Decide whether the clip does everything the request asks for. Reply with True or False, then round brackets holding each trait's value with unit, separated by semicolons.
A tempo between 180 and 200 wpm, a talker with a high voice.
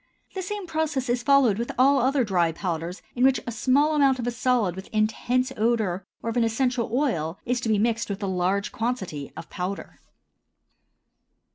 True (185 wpm; 235 Hz)